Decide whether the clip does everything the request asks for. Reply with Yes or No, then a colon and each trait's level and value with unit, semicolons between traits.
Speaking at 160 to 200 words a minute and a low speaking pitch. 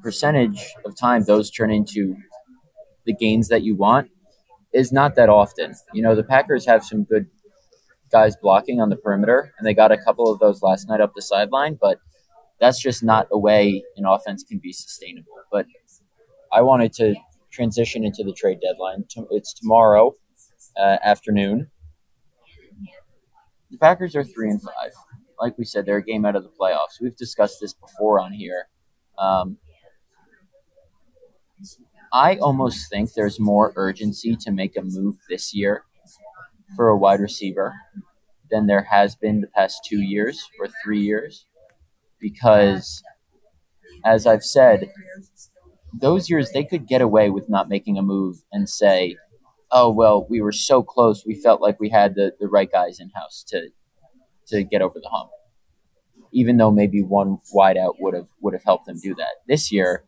Yes: average, 170 wpm; low, 110 Hz